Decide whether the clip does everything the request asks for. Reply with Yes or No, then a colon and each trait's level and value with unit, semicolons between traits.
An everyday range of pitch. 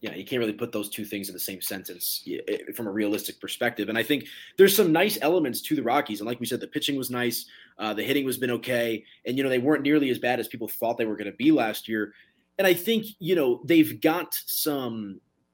No: wide, 6.0 semitones